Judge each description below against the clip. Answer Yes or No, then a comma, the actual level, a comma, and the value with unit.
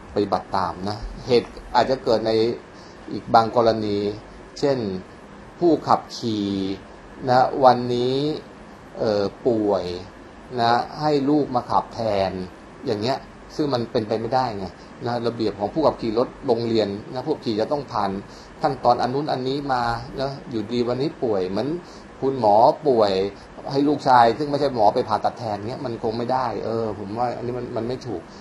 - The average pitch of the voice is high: No, low, 115 Hz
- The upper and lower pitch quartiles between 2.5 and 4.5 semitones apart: Yes, average, 3.8 semitones